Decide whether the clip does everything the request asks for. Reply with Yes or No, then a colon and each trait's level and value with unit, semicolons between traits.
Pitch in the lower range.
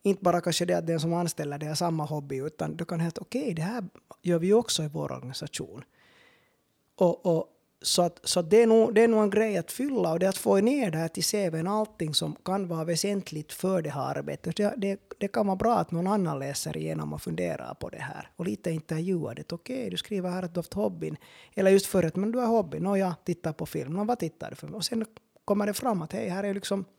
No: medium, 185 Hz